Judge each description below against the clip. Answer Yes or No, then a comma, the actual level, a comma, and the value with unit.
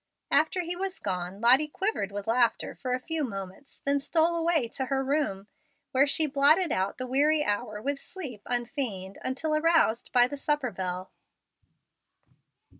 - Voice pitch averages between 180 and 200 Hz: No, very high, 270 Hz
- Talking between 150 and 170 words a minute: Yes, average, 160 wpm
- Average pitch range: No, wide, 5.8 semitones